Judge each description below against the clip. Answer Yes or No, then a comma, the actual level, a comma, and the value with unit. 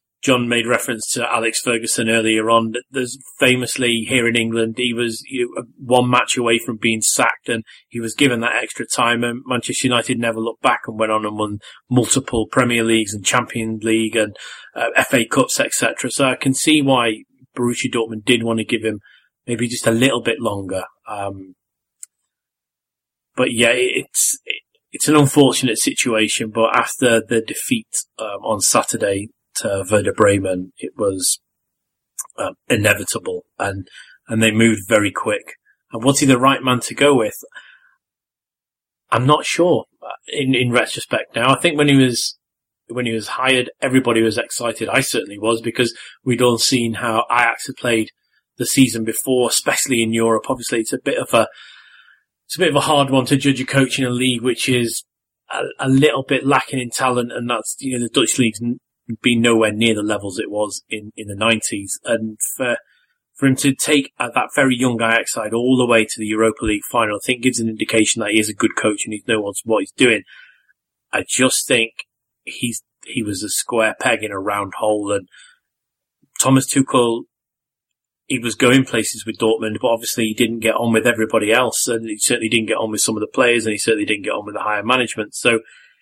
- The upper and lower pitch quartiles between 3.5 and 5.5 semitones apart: No, narrow, 2.5 semitones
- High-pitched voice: No, low, 120 Hz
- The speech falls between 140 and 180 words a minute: No, average, 195 wpm